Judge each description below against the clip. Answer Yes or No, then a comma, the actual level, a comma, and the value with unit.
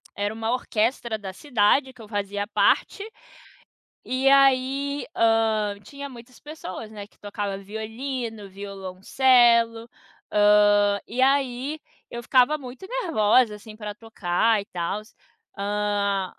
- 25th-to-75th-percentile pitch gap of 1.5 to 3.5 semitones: No, average, 3.9 semitones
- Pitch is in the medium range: No, high, 225 Hz